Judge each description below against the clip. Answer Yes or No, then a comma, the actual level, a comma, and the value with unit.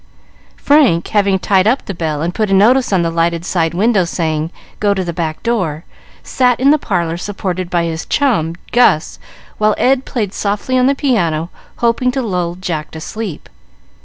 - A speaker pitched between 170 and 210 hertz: Yes, high, 190 Hz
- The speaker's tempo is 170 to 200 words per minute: Yes, average, 185 wpm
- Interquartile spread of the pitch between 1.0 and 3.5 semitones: No, wide, 5.6 semitones